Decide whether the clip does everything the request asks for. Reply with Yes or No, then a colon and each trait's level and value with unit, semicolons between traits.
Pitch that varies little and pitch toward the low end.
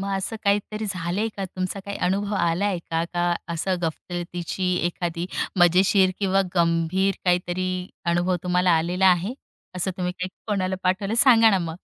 No: narrow, 2.0 semitones; medium, 185 Hz